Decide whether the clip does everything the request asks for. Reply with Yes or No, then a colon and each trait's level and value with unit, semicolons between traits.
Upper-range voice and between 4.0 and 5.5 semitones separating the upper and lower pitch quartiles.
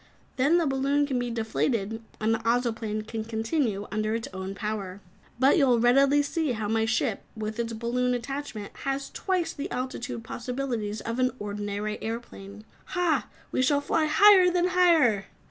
Yes: high, 235 Hz; average, 4.3 semitones